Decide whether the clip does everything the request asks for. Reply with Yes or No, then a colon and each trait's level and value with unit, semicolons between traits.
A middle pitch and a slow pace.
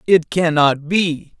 Yes: medium, 165 Hz; slow, 130 wpm